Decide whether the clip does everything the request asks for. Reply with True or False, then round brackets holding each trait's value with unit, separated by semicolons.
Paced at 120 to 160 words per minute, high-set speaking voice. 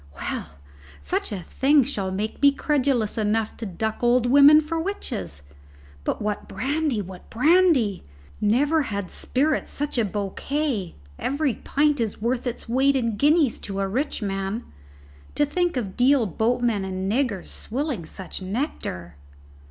True (145 wpm; 240 Hz)